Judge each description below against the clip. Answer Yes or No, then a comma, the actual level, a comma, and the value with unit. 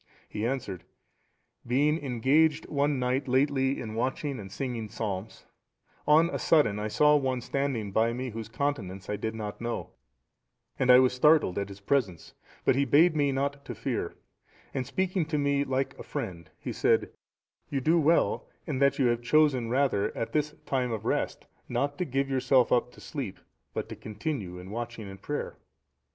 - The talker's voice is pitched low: Yes, low, 130 Hz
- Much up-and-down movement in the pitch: No, average, 4.1 semitones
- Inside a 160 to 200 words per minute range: Yes, average, 180 wpm